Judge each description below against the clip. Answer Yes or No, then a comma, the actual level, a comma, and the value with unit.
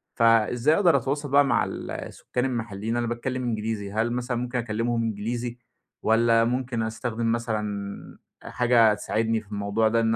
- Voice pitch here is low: Yes, low, 115 Hz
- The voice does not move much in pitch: Yes, narrow, 1.7 semitones